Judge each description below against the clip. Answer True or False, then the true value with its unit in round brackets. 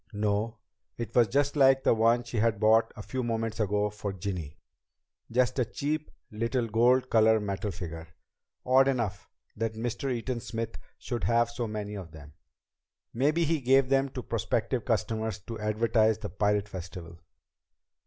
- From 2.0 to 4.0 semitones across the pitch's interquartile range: True (3.1 semitones)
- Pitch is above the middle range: False (115 Hz)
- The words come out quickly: False (160 wpm)